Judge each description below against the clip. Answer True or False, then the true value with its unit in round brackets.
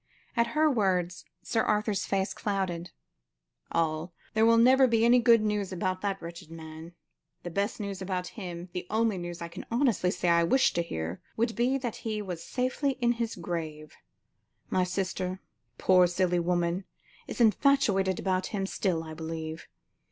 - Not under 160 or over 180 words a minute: True (165 wpm)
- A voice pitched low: False (190 Hz)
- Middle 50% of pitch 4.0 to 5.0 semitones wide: True (4.7 semitones)